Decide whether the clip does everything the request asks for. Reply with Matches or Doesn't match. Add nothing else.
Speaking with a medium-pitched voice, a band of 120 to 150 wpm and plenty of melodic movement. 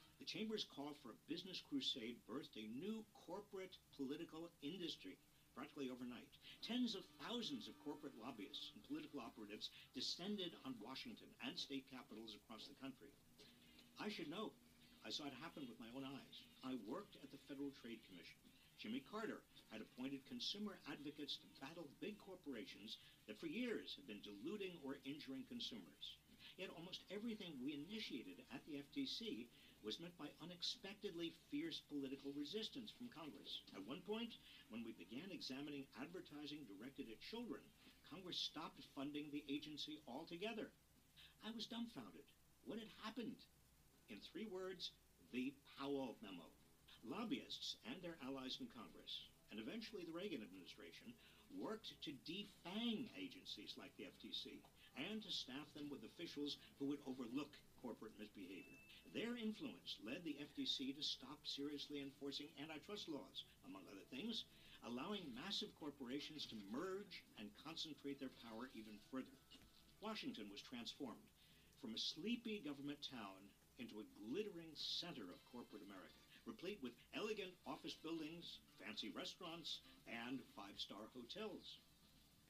Matches